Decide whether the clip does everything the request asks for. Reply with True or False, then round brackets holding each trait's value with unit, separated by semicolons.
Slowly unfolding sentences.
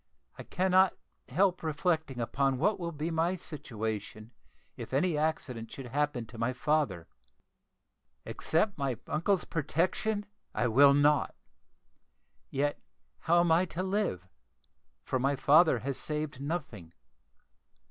True (125 wpm)